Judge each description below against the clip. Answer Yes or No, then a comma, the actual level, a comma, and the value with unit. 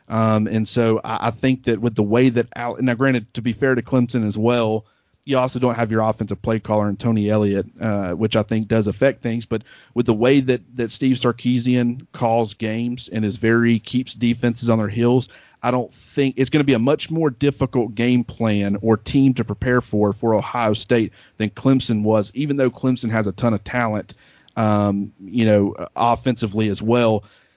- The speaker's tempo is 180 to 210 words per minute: Yes, fast, 205 wpm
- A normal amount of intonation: No, narrow, 2.2 semitones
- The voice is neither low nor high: No, low, 115 Hz